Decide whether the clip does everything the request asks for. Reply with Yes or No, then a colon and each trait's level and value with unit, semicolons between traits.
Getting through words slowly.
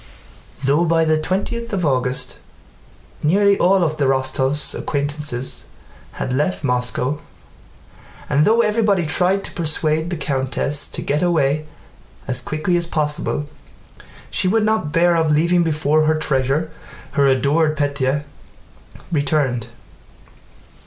Yes: slow, 120 wpm